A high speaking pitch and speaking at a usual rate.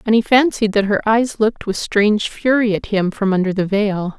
No: high, 210 Hz; fast, 230 wpm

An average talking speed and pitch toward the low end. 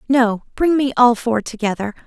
No: average, 175 wpm; high, 240 Hz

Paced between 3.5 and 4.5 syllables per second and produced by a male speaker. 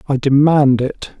Yes: 4.0 syllables/s; male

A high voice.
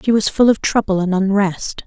Yes: high, 200 Hz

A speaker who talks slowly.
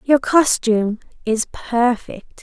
Yes: slow, 100 wpm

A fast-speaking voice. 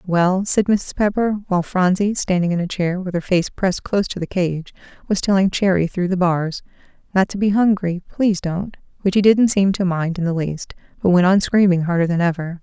Yes: fast, 220 wpm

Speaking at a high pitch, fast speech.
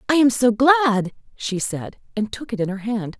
Yes: high, 230 Hz; fast, 225 wpm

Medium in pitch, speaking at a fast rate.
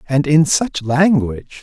No: medium, 145 Hz; average, 145 wpm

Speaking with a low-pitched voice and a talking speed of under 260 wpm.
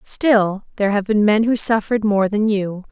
No: high, 210 Hz; fast, 205 wpm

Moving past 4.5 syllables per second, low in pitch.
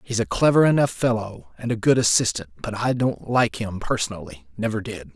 Yes: 5.4 syllables/s; low, 110 Hz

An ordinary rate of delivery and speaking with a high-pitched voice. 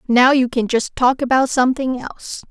Yes: average, 190 wpm; very high, 255 Hz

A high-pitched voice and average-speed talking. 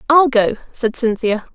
Yes: very high, 250 Hz; average, 155 wpm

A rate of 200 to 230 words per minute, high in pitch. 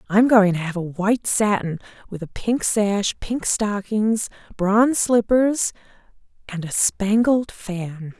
No: average, 140 wpm; high, 205 Hz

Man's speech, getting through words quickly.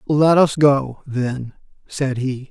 No: male; average, 145 wpm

